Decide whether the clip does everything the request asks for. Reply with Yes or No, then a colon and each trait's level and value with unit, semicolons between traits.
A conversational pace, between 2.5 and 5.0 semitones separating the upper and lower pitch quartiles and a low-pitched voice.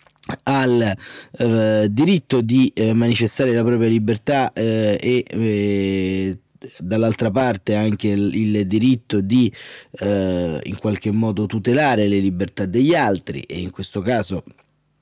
Yes: average, 130 wpm; average, 2.8 semitones; low, 110 Hz